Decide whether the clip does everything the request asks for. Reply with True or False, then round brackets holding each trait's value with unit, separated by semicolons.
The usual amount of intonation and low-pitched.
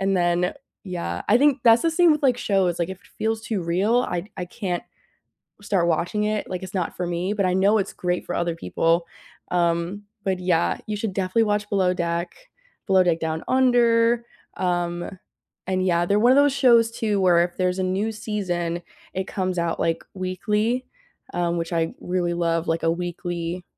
False (3.4 semitones; 185 Hz)